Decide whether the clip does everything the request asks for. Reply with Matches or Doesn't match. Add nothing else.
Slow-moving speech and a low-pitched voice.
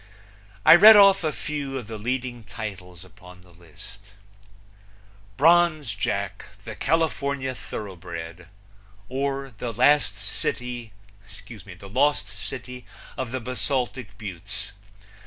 Matches